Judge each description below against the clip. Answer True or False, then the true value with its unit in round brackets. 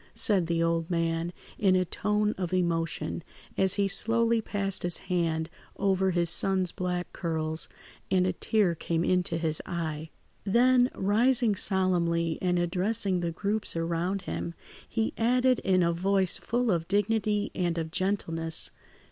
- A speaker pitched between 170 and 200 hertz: True (185 Hz)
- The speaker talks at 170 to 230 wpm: False (150 wpm)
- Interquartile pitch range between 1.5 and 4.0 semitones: True (3.3 semitones)